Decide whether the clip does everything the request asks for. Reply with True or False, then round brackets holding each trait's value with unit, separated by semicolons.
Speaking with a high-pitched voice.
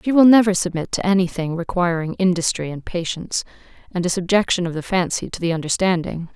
False (180 Hz)